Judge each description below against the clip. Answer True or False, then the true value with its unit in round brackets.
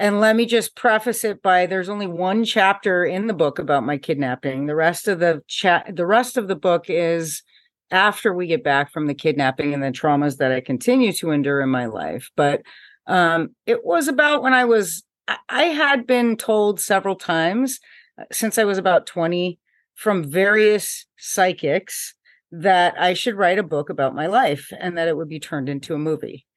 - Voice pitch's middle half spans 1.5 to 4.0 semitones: False (5.6 semitones)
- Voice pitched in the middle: True (180 Hz)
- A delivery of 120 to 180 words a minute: False (200 wpm)